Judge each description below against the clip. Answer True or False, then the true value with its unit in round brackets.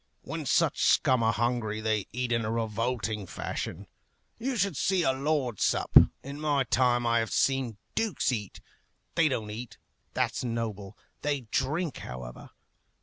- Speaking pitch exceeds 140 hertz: False (120 Hz)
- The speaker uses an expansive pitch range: False (4.1 semitones)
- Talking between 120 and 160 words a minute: True (150 wpm)